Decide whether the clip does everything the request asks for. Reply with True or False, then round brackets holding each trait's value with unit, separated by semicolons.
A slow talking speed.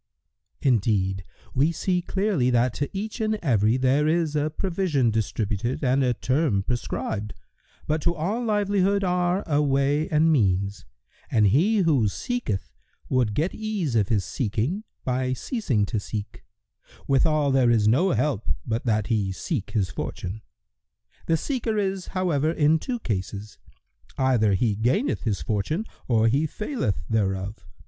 False (150 wpm)